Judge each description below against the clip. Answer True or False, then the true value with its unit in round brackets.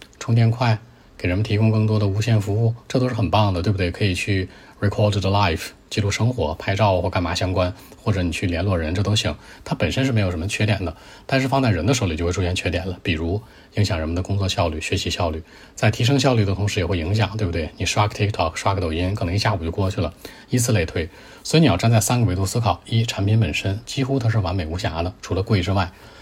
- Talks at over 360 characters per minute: True (400 characters per minute)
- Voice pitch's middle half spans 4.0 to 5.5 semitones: False (3.5 semitones)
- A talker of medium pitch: False (100 Hz)